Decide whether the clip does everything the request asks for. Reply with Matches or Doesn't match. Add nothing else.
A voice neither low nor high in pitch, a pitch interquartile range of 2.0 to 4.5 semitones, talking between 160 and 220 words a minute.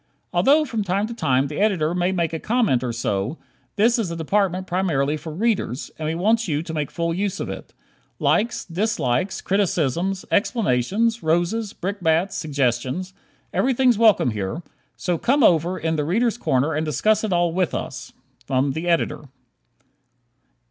Doesn't match